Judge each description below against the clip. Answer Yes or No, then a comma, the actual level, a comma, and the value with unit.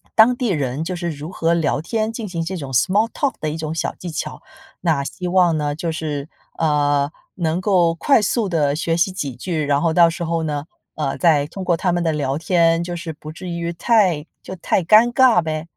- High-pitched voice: No, medium, 165 Hz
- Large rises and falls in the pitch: No, average, 3.2 semitones